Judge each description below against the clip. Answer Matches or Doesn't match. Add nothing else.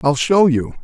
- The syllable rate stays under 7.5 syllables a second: Matches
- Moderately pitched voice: Matches